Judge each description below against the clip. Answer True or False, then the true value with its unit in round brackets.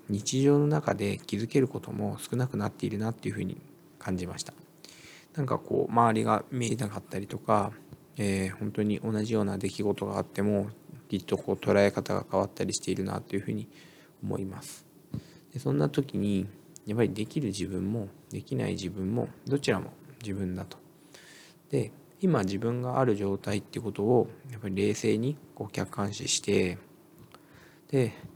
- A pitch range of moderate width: True (4.9 semitones)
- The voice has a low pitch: True (105 Hz)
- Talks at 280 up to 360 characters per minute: True (345 characters per minute)